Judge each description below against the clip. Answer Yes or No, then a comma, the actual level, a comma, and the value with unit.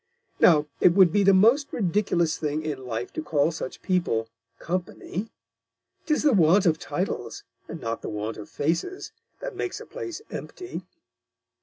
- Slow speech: No, average, 160 wpm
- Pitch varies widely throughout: Yes, wide, 6.0 semitones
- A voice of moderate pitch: Yes, medium, 170 Hz